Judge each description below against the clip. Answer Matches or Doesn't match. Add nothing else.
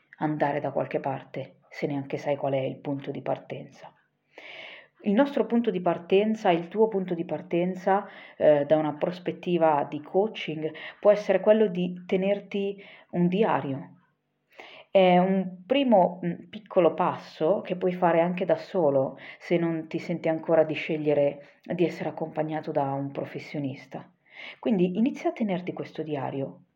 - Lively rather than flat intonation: Doesn't match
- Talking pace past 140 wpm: Matches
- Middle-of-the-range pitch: Matches